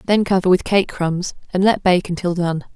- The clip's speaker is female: Yes, female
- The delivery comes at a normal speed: No, fast, 220 wpm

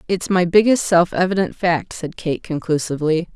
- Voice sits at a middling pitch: Yes, medium, 175 Hz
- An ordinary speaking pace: Yes, average, 160 wpm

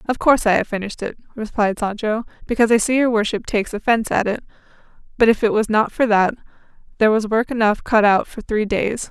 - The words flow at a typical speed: No, fast, 220 wpm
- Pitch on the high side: Yes, high, 220 Hz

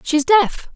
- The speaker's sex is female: Yes, female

